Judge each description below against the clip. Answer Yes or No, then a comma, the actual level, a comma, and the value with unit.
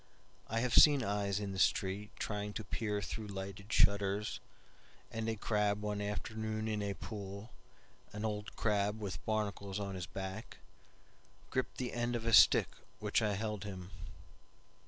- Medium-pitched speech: No, low, 105 Hz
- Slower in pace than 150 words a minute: Yes, average, 140 wpm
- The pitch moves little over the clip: Yes, narrow, 1.7 semitones